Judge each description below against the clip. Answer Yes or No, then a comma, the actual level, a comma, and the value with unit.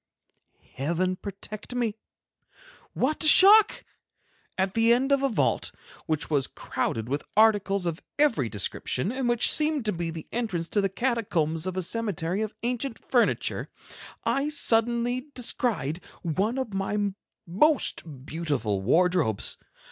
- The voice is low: No, high, 205 Hz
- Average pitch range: No, wide, 6.6 semitones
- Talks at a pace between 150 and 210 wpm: No, slow, 135 wpm